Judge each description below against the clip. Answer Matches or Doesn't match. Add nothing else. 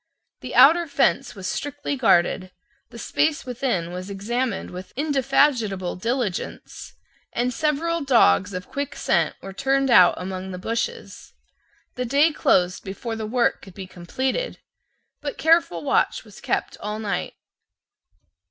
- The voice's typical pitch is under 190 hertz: Doesn't match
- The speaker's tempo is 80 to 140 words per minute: Matches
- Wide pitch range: Matches